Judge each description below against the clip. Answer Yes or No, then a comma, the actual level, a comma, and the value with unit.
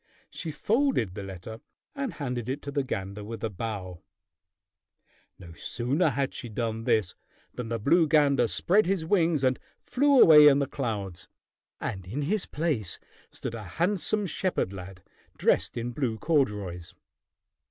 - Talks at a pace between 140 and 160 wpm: Yes, average, 155 wpm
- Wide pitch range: Yes, wide, 7.4 semitones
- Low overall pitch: Yes, low, 125 Hz